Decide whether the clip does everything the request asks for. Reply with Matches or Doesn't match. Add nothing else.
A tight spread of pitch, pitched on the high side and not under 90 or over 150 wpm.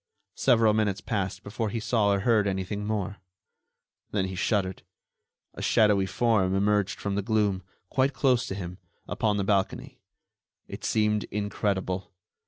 Doesn't match